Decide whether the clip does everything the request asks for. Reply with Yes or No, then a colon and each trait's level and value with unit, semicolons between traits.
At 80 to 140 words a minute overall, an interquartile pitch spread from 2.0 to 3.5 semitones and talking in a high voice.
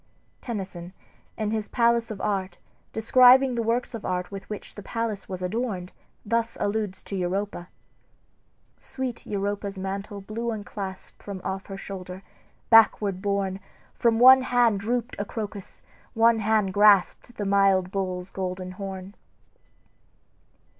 Yes: slow, 135 wpm; average, 3.0 semitones; high, 205 Hz